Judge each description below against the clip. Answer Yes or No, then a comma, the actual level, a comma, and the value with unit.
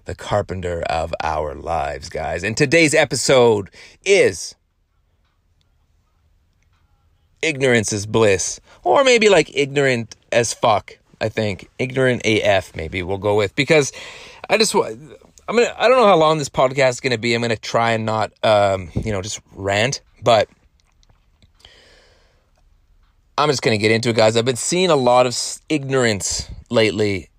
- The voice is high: No, low, 110 Hz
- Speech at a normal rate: Yes, average, 155 wpm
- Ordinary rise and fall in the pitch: No, wide, 6.8 semitones